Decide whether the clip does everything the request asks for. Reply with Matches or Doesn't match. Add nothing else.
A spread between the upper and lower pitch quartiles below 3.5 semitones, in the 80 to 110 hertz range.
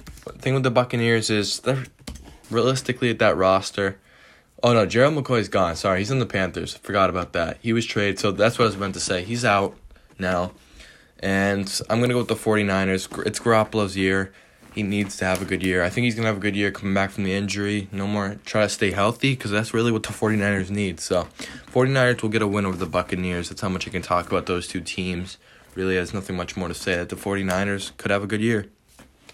Matches